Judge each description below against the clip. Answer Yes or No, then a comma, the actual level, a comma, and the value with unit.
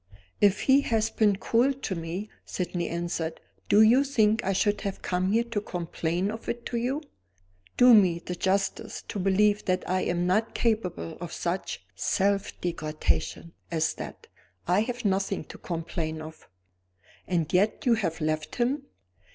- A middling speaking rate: Yes, average, 160 wpm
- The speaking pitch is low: No, high, 195 Hz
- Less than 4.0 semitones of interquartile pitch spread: No, average, 4.4 semitones